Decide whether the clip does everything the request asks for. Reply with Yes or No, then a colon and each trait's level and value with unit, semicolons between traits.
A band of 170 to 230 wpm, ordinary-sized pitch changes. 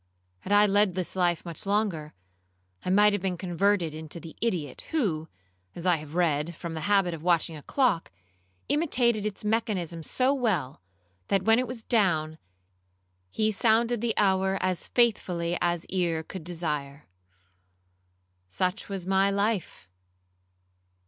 No: average, 145 wpm; average, 4.0 semitones